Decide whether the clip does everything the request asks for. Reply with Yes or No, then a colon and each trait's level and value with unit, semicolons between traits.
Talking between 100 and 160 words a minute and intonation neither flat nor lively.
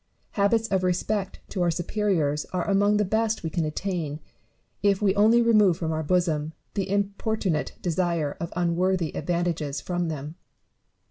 Yes: average, 150 wpm; average, 3.8 semitones